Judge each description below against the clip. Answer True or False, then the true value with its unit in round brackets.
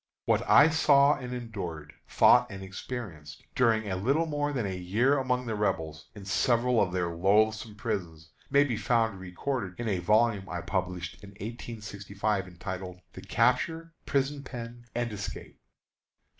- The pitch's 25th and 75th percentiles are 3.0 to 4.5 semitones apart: False (5.0 semitones)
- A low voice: True (105 Hz)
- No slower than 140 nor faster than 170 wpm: True (155 wpm)